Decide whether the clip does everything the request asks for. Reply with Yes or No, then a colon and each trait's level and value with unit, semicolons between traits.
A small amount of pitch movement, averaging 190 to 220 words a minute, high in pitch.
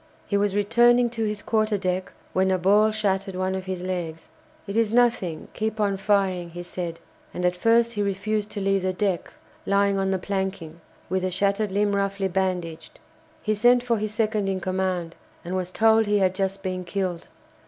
Yes: narrow, 2.3 semitones; average, 195 wpm; high, 195 Hz